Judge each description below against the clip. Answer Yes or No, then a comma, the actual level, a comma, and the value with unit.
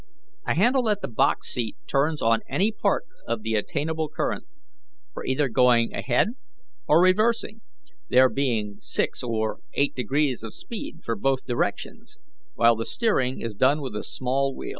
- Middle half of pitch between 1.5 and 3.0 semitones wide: No, wide, 5.6 semitones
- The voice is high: No, low, 130 Hz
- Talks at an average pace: Yes, average, 160 wpm